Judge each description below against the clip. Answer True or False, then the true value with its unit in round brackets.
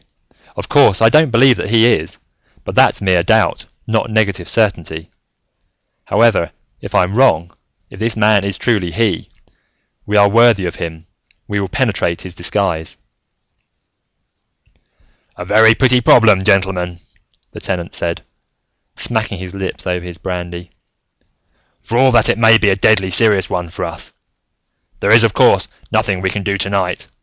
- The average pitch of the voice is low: True (100 Hz)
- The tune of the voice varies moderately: True (3.9 semitones)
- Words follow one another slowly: False (155 wpm)